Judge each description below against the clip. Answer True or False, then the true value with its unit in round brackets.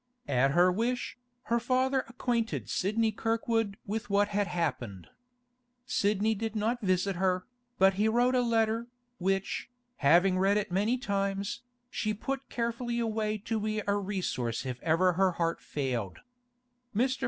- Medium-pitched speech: False (205 Hz)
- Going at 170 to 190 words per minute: False (145 wpm)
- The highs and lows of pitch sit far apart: False (3.8 semitones)